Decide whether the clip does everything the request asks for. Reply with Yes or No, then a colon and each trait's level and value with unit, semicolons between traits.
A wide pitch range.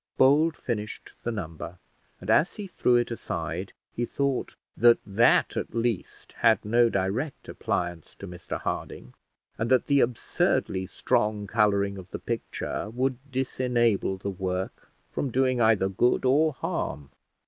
No: average, 4.7 semitones